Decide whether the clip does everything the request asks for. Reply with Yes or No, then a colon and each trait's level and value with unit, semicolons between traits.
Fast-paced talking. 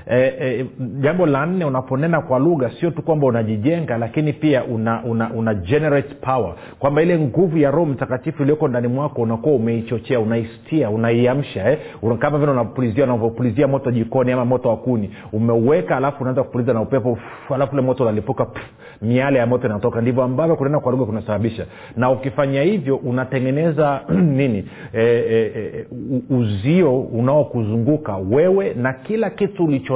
Yes: fast, 145 wpm